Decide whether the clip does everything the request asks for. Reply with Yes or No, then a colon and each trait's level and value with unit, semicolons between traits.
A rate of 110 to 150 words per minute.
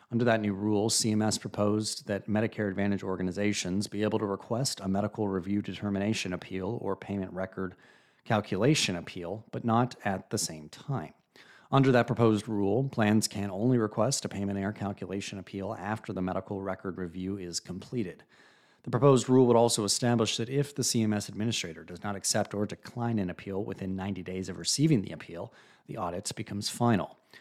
No: average, 175 wpm